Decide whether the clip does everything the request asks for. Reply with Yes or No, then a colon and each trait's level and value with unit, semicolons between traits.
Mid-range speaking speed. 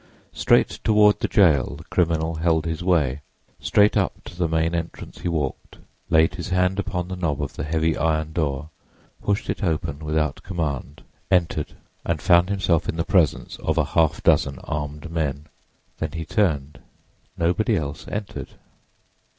Yes: average, 160 wpm